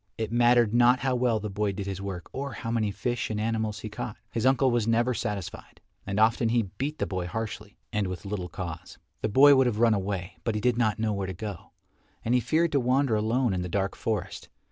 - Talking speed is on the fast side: Yes, fast, 235 wpm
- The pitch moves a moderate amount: Yes, average, 3.4 semitones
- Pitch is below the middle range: Yes, low, 110 Hz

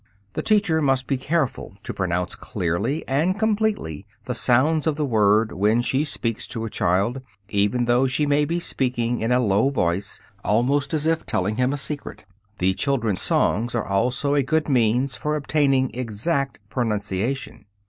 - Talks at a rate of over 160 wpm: Yes, average, 170 wpm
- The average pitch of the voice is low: Yes, low, 125 Hz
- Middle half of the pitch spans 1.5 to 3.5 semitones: No, average, 5.1 semitones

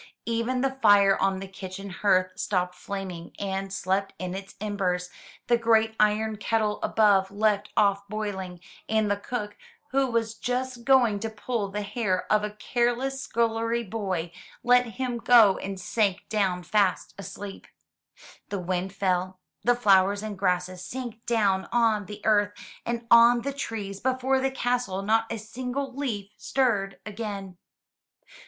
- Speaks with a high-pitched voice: Yes, high, 210 Hz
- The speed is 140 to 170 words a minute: Yes, average, 150 wpm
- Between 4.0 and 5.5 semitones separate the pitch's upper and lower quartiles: No, average, 3.3 semitones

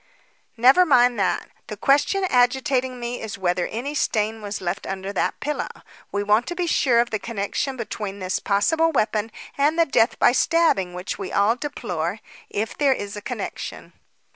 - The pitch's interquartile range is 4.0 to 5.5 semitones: Yes, average, 5.2 semitones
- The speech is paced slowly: No, average, 175 wpm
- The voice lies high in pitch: Yes, high, 230 Hz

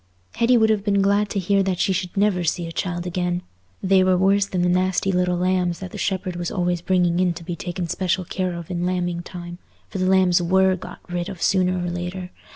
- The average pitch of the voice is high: No, medium, 180 Hz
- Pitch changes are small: Yes, narrow, 1.3 semitones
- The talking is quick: Yes, fast, 235 wpm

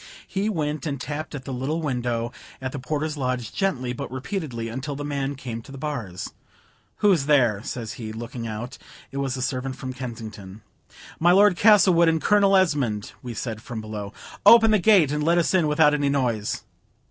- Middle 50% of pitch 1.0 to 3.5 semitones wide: No, average, 4.9 semitones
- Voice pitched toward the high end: No, low, 135 Hz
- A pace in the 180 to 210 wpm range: Yes, average, 190 wpm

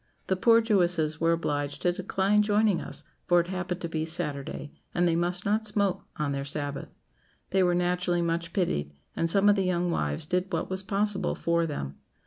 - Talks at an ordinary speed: Yes, average, 195 wpm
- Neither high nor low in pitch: Yes, medium, 175 Hz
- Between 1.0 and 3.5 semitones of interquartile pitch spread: Yes, average, 3.2 semitones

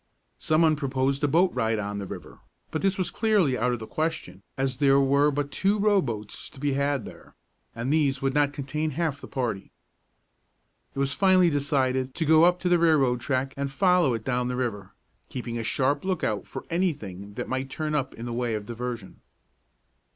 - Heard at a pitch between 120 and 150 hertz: Yes, low, 135 Hz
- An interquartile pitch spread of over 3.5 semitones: Yes, average, 4.1 semitones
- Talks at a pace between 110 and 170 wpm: No, fast, 205 wpm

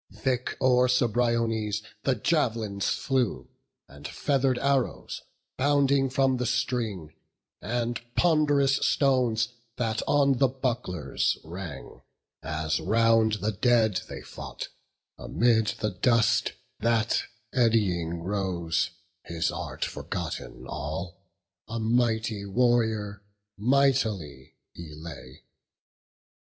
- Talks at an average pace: No, slow, 95 wpm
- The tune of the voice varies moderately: Yes, average, 4.7 semitones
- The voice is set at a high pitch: No, low, 115 Hz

